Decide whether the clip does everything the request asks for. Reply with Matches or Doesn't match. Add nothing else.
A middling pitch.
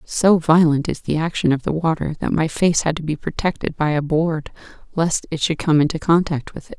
Matches